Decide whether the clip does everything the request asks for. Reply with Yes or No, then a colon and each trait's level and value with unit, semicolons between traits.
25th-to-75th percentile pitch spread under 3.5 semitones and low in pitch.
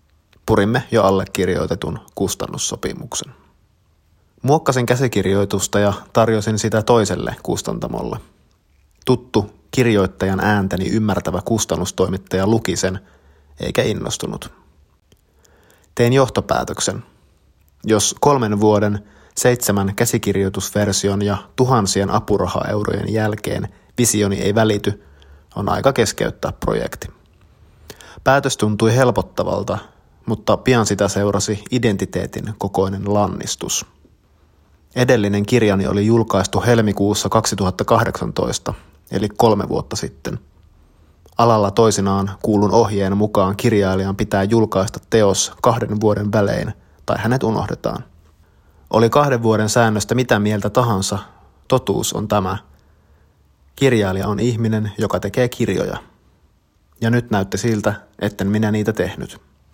Yes: average, 2.9 semitones; low, 100 Hz